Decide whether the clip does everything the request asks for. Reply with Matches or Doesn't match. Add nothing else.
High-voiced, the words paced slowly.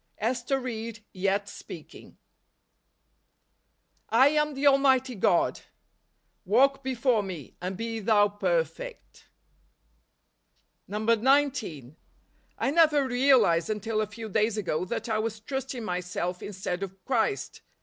Matches